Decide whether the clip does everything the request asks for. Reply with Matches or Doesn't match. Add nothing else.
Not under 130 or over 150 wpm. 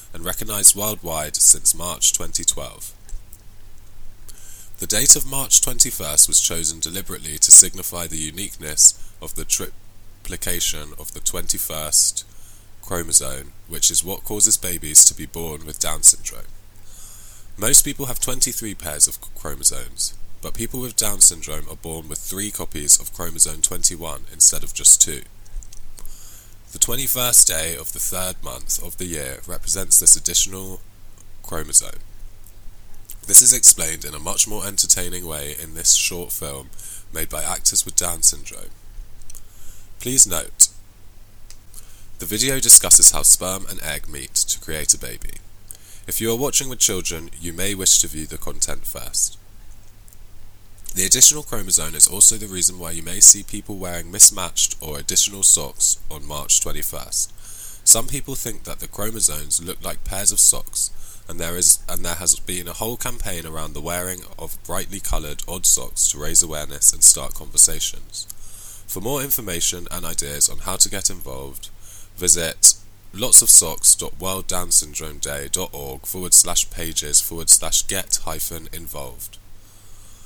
Matches